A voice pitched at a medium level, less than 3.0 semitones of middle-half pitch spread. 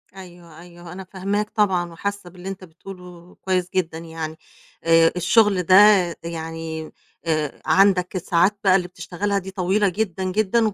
Yes: medium, 180 Hz; narrow, 2.5 semitones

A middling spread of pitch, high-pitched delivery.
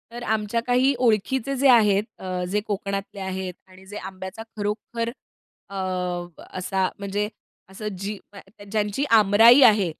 Yes: average, 3.1 semitones; high, 205 Hz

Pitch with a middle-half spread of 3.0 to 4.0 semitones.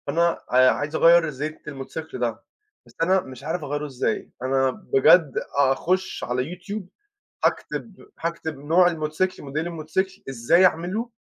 No: average, 4.5 semitones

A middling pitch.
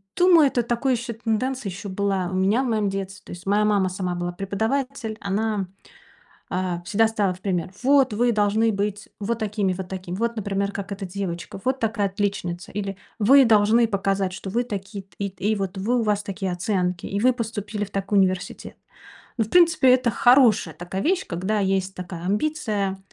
No: high, 205 Hz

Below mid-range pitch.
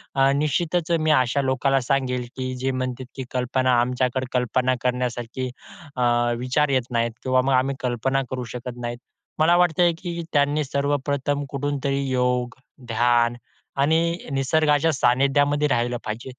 Yes: low, 130 Hz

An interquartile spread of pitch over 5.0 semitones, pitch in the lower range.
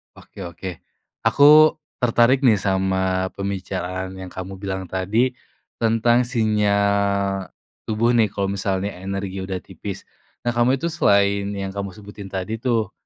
No: average, 2.9 semitones; low, 100 Hz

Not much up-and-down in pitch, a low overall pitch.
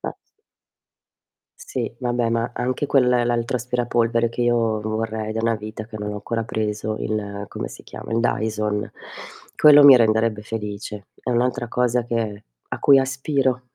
Yes: narrow, 2.3 semitones; low, 115 Hz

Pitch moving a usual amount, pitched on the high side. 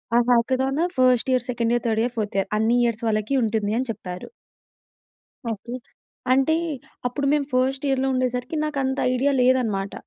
Yes: average, 3.0 semitones; high, 245 Hz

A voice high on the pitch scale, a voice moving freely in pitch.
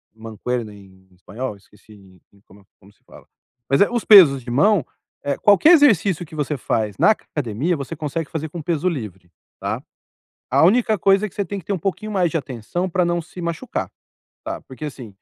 No: medium, 150 Hz; wide, 8.4 semitones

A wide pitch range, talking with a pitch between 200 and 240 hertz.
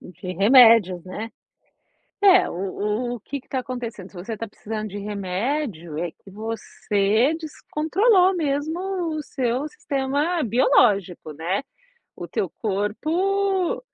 Yes: wide, 6.9 semitones; high, 230 Hz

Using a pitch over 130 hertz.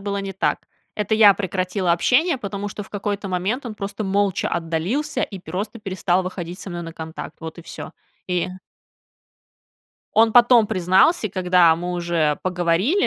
Yes: high, 190 Hz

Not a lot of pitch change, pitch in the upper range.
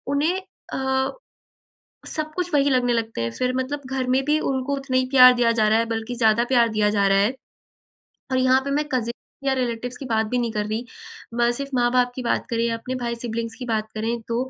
Yes: narrow, 2.3 semitones; high, 245 Hz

